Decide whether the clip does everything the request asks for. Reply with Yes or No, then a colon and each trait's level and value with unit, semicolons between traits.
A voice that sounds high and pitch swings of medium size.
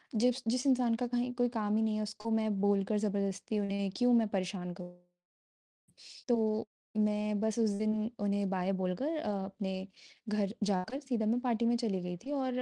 Yes: high, 215 Hz; average, 3.0 semitones